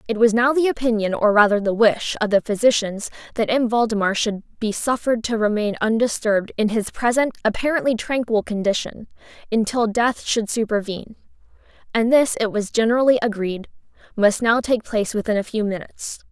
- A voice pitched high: Yes, high, 220 Hz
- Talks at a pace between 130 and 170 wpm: Yes, average, 160 wpm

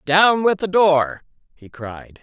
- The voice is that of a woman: No, male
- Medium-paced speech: Yes, average, 160 wpm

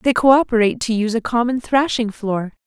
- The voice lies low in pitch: No, high, 230 Hz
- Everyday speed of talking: Yes, average, 180 wpm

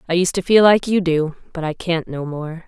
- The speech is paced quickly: Yes, fast, 270 wpm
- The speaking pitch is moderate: Yes, medium, 170 Hz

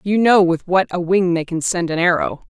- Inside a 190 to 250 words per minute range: No, fast, 260 wpm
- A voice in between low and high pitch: Yes, medium, 180 Hz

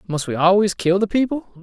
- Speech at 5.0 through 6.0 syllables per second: Yes, 5.8 syllables/s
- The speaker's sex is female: No, male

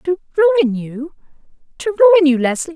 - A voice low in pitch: No, very high, 305 Hz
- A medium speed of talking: No, slow, 130 wpm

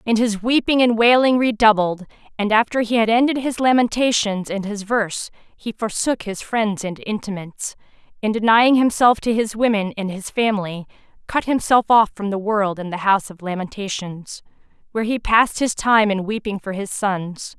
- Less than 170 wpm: No, average, 175 wpm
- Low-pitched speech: No, high, 215 Hz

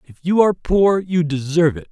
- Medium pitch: Yes, medium, 170 Hz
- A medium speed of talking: No, fast, 220 wpm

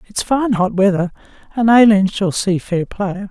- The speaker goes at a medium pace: Yes, average, 180 wpm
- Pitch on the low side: No, high, 200 Hz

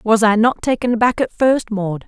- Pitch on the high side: Yes, high, 225 Hz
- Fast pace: Yes, fast, 230 wpm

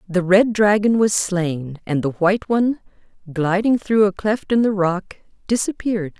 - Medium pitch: No, high, 200 Hz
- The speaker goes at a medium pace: Yes, average, 165 wpm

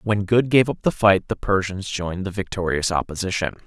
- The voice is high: No, low, 100 Hz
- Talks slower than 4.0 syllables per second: No, 5.5 syllables/s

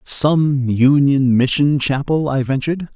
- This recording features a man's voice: Yes, male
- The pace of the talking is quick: No, slow, 120 wpm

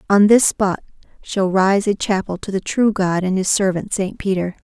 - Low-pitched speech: No, high, 195 Hz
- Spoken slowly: No, fast, 205 wpm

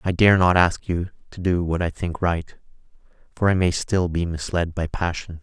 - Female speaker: No, male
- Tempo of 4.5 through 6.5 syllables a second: Yes, 4.8 syllables/s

